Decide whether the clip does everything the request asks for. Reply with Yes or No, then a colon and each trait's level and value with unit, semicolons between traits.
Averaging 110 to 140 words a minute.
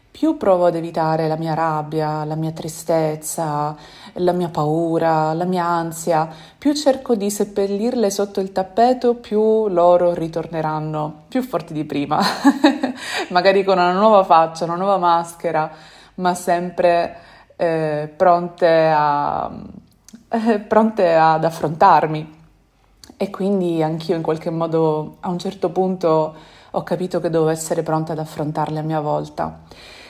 Yes: average, 135 wpm